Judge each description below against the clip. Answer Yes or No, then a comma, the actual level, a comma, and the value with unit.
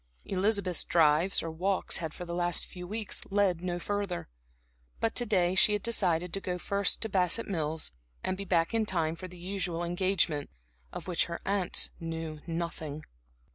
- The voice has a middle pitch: Yes, medium, 180 Hz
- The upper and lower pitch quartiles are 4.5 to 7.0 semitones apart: No, average, 3.0 semitones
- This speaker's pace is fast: No, average, 175 wpm